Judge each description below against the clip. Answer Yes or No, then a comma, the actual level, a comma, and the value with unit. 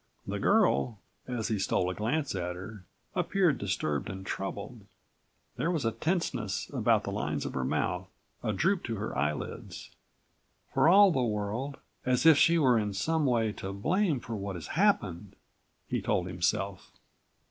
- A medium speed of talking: Yes, average, 165 wpm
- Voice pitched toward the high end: No, low, 110 Hz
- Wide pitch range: Yes, wide, 8.0 semitones